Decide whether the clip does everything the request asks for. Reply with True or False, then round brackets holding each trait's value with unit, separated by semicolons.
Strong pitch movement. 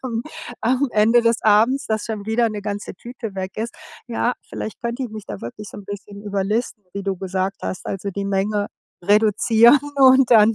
False (2.8 semitones)